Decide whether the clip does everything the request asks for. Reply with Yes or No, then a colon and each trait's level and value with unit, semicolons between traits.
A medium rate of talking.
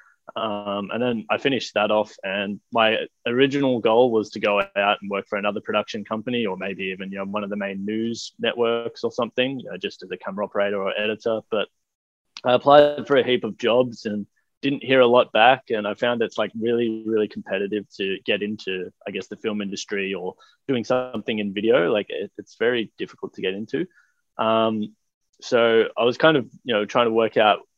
No: fast, 210 wpm